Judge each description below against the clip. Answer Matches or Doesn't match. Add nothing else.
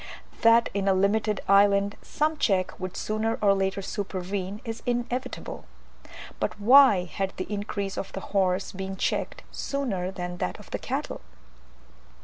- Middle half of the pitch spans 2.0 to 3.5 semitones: Matches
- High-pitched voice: Matches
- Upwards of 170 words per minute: Doesn't match